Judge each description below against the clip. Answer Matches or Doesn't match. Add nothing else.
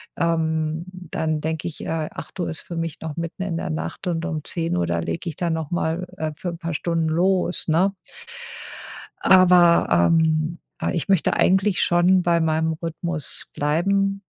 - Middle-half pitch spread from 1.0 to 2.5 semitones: Matches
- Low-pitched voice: Doesn't match